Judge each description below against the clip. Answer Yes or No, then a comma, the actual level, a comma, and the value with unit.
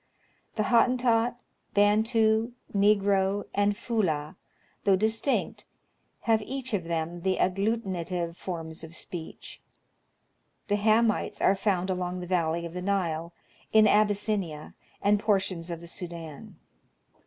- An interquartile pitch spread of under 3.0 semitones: No, average, 4.0 semitones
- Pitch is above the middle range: Yes, high, 195 Hz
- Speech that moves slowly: Yes, slow, 120 wpm